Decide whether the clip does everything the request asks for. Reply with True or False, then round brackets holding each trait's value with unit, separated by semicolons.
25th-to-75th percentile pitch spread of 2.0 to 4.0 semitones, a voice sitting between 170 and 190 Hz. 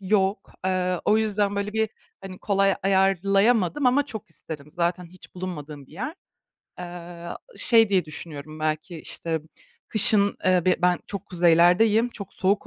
True (2.9 semitones; 185 Hz)